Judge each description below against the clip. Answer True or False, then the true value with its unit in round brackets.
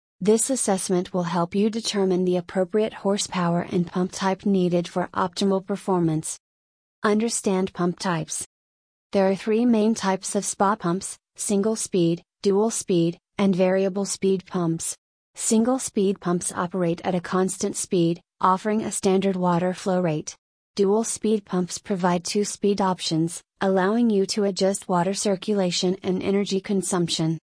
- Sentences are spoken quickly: False (140 wpm)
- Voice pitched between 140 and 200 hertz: True (190 Hz)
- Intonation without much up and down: True (2.2 semitones)